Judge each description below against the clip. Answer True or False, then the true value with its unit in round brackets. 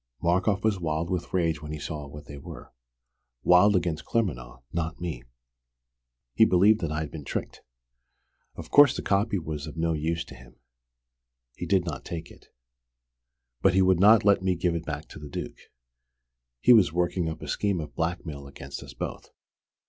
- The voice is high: False (85 Hz)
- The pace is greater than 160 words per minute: True (180 wpm)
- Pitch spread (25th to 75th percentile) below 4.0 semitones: True (3.5 semitones)